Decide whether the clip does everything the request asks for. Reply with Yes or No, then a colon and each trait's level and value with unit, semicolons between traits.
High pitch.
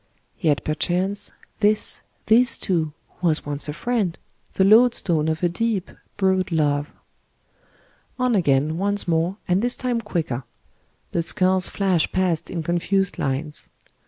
No: medium, 180 Hz